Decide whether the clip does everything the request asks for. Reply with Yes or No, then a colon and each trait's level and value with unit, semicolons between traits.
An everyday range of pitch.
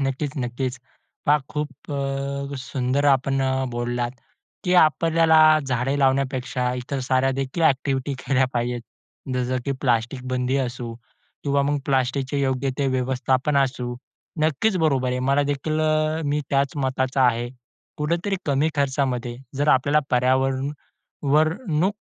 No: narrow, 2.2 semitones